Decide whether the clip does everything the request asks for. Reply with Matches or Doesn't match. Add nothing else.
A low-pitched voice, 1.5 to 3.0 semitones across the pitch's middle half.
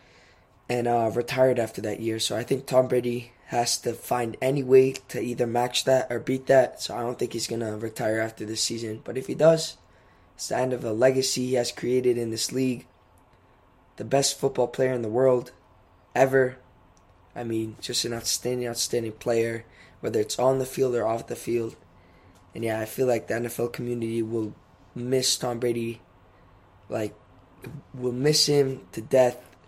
Matches